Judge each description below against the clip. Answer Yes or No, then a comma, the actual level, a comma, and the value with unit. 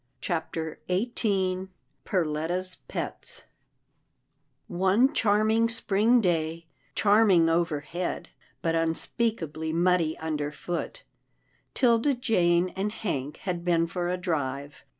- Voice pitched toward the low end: No, medium, 180 Hz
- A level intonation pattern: No, average, 4.1 semitones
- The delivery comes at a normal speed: No, slow, 95 wpm